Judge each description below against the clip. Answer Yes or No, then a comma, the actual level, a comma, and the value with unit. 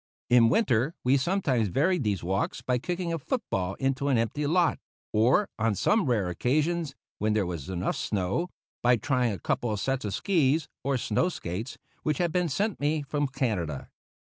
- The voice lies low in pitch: Yes, low, 130 Hz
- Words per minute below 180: No, average, 185 wpm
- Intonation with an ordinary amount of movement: No, wide, 6.7 semitones